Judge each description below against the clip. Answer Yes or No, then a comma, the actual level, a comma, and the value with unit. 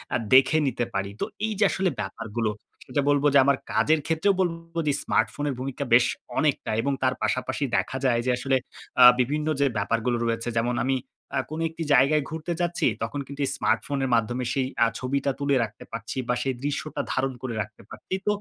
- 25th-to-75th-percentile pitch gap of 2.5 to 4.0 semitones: Yes, average, 3.6 semitones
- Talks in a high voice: No, low, 135 Hz